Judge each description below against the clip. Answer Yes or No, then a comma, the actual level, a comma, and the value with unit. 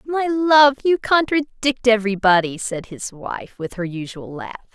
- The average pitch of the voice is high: Yes, high, 235 Hz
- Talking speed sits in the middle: Yes, average, 165 wpm